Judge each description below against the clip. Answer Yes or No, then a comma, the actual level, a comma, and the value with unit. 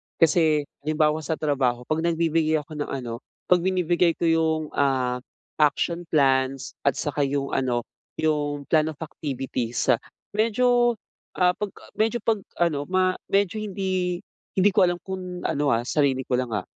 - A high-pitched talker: No, medium, 155 Hz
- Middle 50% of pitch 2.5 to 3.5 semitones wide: No, average, 4.7 semitones